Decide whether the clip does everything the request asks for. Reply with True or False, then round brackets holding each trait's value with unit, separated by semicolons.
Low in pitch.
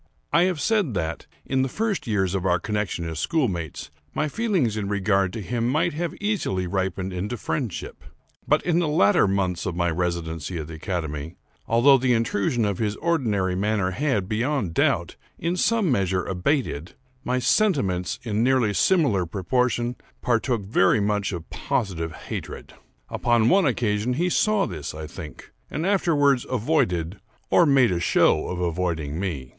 True (105 Hz)